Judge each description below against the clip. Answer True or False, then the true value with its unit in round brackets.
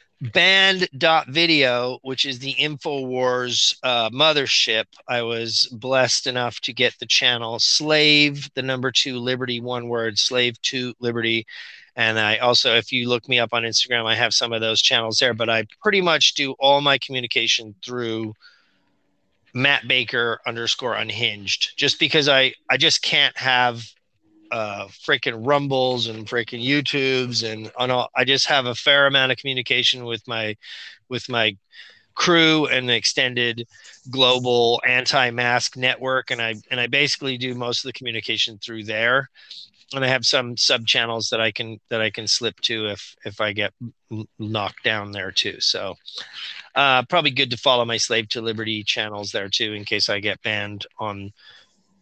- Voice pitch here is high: False (120 Hz)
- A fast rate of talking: False (165 wpm)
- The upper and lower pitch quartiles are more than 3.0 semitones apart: False (2.6 semitones)